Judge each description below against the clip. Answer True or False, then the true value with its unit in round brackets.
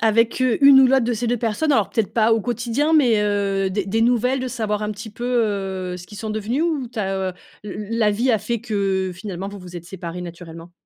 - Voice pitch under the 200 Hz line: False (215 Hz)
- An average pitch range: True (3.6 semitones)